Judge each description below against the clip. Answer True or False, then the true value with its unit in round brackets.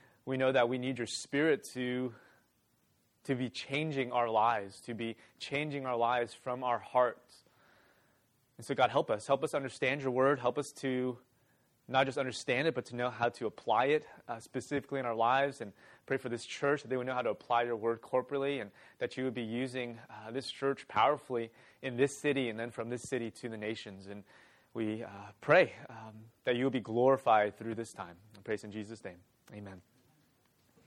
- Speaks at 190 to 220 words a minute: True (200 wpm)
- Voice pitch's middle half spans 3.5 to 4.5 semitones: False (2.7 semitones)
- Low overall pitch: True (125 Hz)